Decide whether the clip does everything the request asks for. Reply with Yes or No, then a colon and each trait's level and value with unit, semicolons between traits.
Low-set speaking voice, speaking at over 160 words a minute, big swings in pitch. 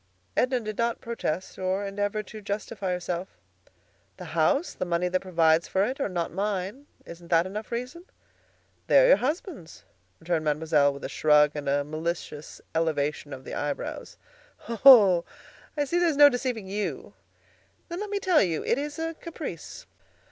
No: high, 195 Hz; average, 170 wpm; wide, 7.7 semitones